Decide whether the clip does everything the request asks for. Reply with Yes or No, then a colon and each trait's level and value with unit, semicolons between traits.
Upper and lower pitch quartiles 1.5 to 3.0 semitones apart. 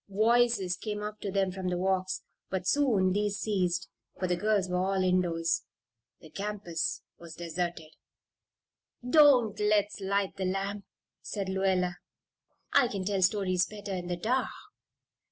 Yes: narrow, 2.4 semitones